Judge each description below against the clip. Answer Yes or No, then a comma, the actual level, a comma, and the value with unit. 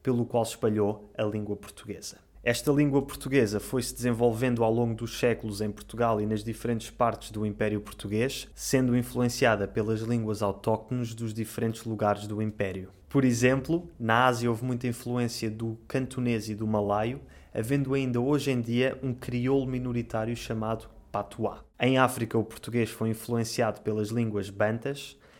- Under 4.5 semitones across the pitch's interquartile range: Yes, narrow, 2.5 semitones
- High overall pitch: No, low, 115 Hz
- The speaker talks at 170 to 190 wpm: No, average, 155 wpm